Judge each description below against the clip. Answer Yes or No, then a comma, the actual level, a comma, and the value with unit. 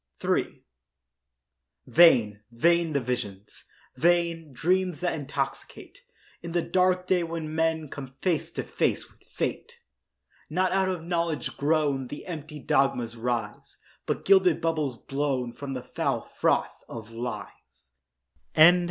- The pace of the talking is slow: Yes, slow, 125 wpm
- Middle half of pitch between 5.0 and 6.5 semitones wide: Yes, average, 5.3 semitones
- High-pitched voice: No, medium, 155 Hz